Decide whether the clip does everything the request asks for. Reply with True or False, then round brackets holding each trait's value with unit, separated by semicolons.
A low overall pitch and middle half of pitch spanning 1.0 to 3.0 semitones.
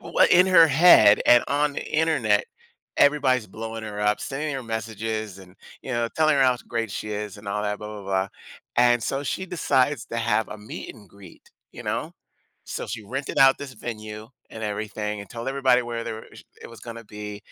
False (115 Hz; 4.2 semitones)